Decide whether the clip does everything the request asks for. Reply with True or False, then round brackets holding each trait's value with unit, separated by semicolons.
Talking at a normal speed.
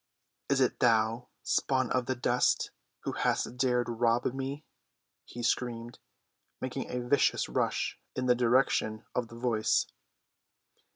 False (130 wpm)